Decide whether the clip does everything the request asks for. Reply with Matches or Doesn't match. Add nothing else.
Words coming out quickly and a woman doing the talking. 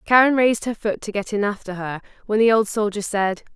Matches